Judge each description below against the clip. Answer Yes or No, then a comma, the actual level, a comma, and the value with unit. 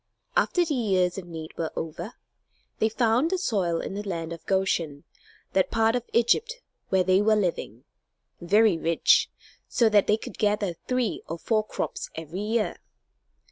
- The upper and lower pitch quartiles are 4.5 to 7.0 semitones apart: Yes, average, 4.8 semitones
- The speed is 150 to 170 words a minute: Yes, average, 165 wpm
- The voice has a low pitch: No, high, 200 Hz